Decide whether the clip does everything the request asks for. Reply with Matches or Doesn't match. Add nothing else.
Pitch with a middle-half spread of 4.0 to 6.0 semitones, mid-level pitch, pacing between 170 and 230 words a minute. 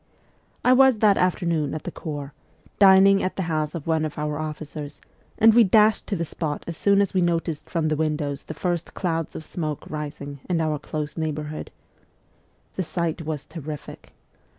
Doesn't match